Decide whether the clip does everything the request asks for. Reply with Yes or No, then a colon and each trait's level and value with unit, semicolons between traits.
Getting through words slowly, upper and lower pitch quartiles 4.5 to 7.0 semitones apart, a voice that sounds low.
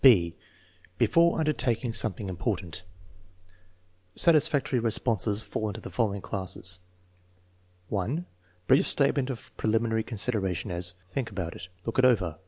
Yes: slow, 125 wpm; average, 5.2 semitones; low, 110 Hz